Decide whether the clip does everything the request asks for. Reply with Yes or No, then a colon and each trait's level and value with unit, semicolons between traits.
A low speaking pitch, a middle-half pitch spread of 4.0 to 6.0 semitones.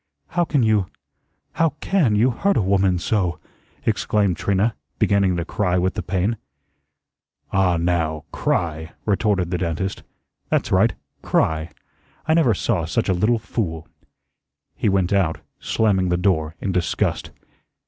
No: very low, 95 Hz; average, 3.5 semitones